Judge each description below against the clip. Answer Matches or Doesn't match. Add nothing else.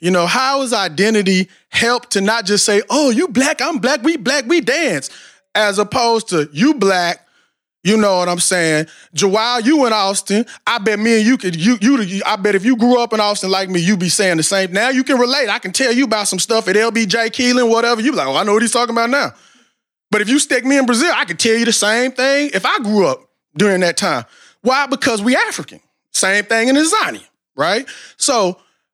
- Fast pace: Matches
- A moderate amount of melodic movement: Matches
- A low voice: Doesn't match